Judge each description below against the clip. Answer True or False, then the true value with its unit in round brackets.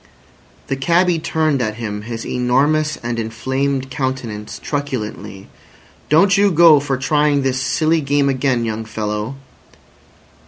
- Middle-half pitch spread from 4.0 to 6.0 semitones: True (4.7 semitones)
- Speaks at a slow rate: True (125 wpm)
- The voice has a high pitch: False (135 Hz)